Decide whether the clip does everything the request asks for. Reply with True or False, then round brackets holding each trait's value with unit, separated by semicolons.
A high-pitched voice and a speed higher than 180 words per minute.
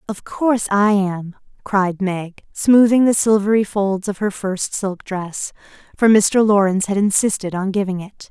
False (200 Hz; 165 wpm)